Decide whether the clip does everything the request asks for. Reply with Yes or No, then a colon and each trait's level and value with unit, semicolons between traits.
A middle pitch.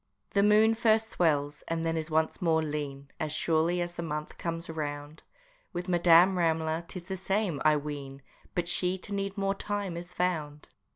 Yes: medium, 170 Hz